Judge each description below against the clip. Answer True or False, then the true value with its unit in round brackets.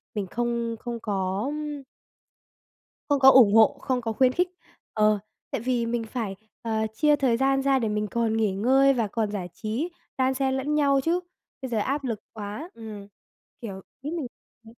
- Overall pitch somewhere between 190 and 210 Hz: False (235 Hz)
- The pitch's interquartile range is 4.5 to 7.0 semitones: False (3.9 semitones)